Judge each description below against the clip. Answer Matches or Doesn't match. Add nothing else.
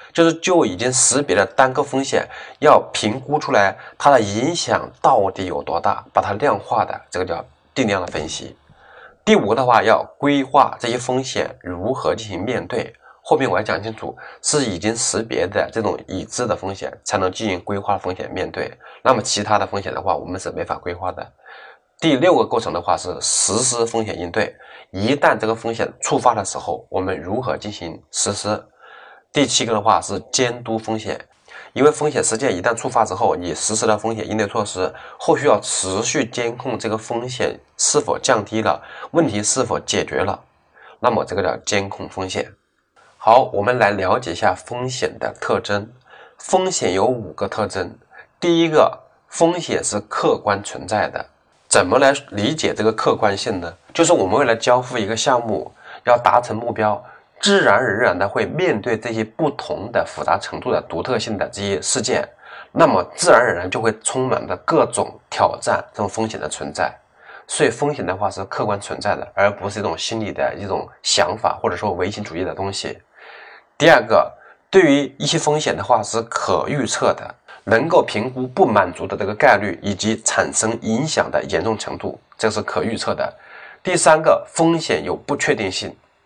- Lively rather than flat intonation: Doesn't match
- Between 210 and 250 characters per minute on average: Doesn't match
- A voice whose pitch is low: Matches